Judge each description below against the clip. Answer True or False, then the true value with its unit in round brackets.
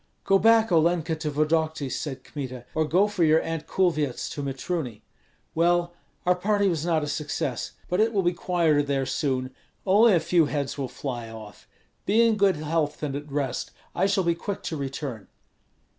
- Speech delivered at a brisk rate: False (185 wpm)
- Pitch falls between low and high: True (160 Hz)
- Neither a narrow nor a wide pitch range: True (4.2 semitones)